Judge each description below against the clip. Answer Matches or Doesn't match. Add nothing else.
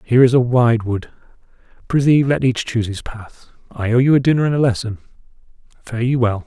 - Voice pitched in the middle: Doesn't match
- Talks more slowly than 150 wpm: Doesn't match